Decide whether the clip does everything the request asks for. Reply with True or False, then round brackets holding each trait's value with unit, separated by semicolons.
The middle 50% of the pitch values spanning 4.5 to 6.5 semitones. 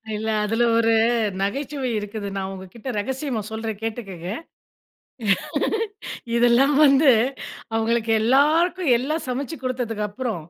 False (3.9 semitones)